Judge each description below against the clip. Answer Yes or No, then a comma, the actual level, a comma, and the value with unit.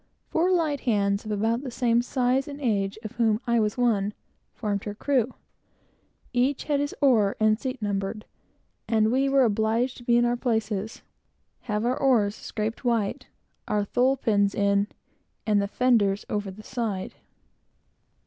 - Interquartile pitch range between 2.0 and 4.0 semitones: Yes, average, 3.4 semitones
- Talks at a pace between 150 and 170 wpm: Yes, average, 160 wpm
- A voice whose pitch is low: No, high, 225 Hz